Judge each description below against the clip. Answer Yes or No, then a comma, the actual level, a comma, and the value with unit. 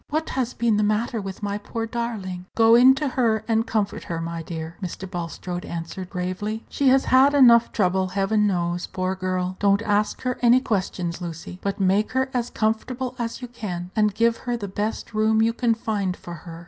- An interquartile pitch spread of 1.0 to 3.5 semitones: No, average, 4.1 semitones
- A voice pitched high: Yes, high, 210 Hz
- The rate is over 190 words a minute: Yes, average, 200 wpm